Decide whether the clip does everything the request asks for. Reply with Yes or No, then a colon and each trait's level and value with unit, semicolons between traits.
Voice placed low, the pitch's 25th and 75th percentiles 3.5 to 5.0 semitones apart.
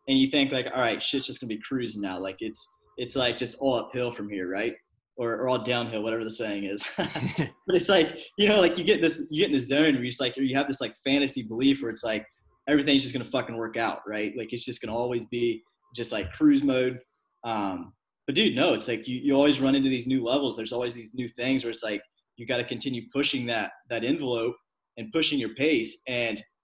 No: low, 125 Hz; average, 3.0 semitones